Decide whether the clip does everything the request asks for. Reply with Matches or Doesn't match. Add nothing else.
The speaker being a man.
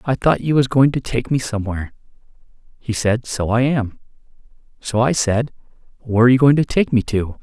Matches